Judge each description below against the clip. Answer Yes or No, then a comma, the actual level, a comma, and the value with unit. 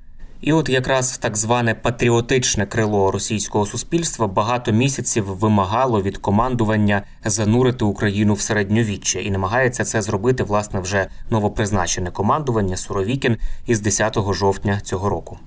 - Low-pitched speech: Yes, low, 105 Hz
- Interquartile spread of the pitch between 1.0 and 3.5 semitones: Yes, average, 3.1 semitones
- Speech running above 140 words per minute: No, average, 125 wpm